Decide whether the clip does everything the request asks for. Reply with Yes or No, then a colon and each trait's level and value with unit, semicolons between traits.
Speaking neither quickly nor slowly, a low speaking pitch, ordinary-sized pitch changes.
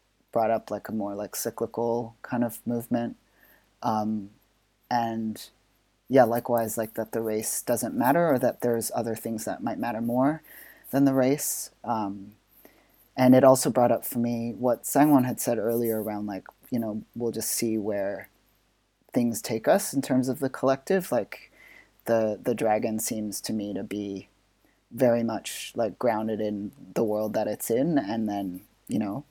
No: average, 170 wpm; low, 115 Hz; narrow, 2.0 semitones